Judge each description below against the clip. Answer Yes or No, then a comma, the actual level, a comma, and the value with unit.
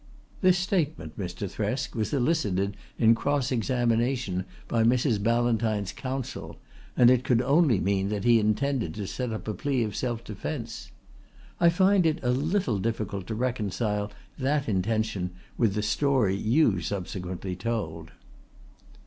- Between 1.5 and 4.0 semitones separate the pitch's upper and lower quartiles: No, average, 4.5 semitones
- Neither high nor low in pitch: No, low, 115 Hz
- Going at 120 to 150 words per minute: Yes, average, 145 wpm